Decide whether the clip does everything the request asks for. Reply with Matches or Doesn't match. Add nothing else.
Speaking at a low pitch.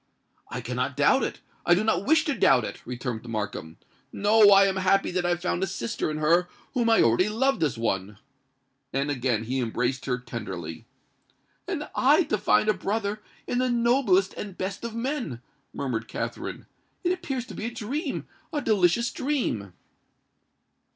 Doesn't match